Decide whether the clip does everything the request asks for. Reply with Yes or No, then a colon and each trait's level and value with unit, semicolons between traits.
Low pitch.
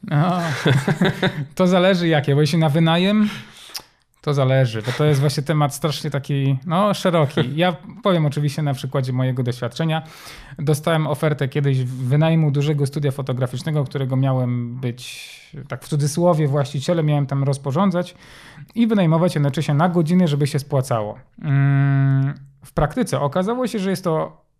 No: medium, 150 Hz